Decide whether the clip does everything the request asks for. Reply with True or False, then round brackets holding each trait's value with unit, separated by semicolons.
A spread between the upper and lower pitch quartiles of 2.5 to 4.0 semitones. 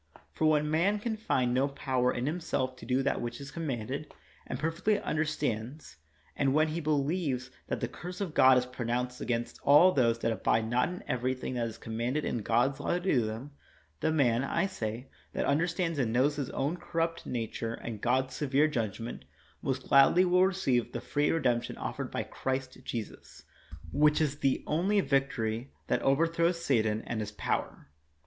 False (4.6 semitones)